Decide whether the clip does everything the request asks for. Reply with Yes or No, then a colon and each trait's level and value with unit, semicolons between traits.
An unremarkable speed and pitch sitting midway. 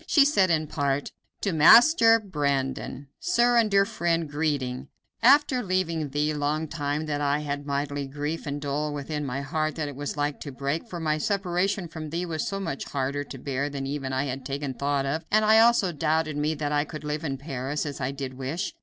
No: fast, 210 wpm; medium, 150 Hz